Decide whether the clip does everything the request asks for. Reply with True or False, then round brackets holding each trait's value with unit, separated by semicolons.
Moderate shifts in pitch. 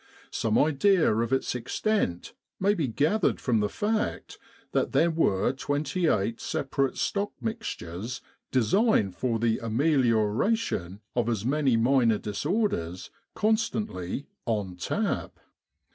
False (8.7 semitones)